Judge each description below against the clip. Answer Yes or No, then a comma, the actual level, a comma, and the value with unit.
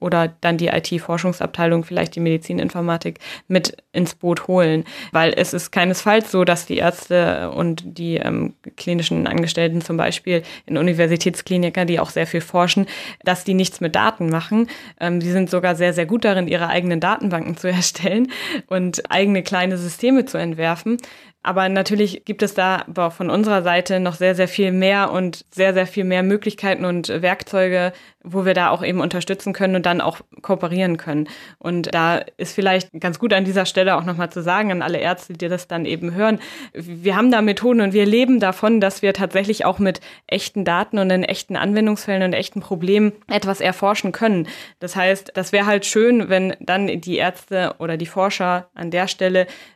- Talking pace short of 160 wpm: No, average, 185 wpm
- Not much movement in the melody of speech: Yes, narrow, 2.2 semitones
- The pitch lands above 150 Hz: Yes, medium, 185 Hz